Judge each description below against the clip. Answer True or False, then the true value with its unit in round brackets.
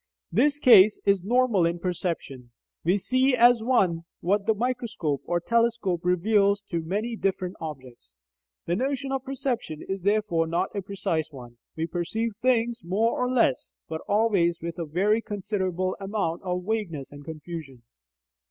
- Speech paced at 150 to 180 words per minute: True (155 wpm)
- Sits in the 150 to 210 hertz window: True (190 Hz)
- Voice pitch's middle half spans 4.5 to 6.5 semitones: True (5.2 semitones)